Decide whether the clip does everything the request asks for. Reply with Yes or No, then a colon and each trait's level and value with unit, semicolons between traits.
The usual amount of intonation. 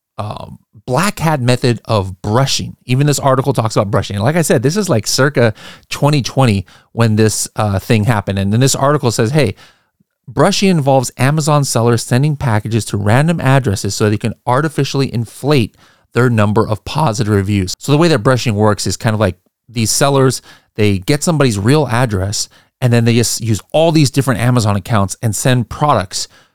Yes: average, 4.4 semitones